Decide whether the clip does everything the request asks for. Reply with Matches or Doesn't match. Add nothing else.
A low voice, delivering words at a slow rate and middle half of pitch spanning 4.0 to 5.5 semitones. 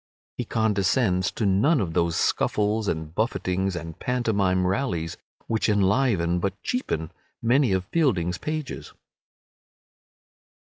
Matches